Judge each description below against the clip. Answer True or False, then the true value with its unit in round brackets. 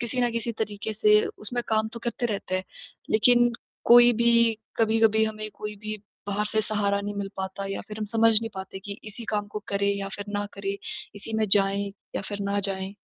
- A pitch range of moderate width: False (1.8 semitones)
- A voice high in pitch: True (210 Hz)